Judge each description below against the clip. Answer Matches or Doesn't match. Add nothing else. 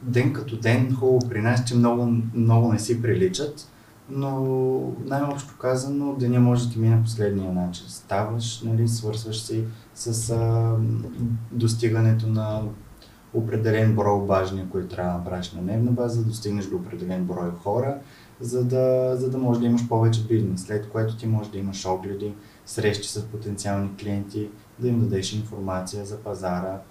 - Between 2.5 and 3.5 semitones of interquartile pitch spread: Matches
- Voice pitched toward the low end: Matches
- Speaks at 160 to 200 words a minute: Matches